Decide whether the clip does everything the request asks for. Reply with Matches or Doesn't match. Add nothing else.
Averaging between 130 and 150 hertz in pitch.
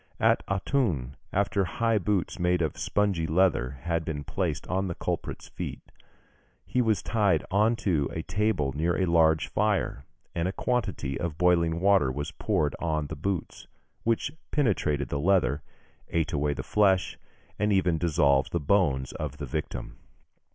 Doesn't match